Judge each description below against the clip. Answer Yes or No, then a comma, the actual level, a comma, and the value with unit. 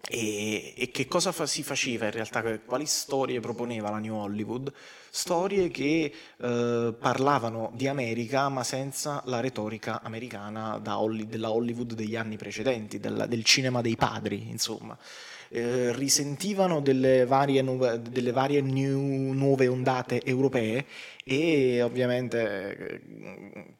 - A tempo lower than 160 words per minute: Yes, average, 135 wpm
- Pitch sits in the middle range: No, low, 125 Hz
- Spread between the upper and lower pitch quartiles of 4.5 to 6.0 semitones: No, average, 3.3 semitones